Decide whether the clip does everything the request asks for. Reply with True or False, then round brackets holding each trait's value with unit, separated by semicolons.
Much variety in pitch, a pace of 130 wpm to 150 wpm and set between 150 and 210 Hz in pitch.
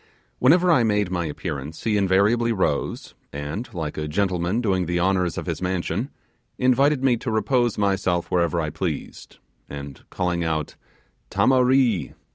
False (5.7 semitones; 145 wpm; 95 Hz)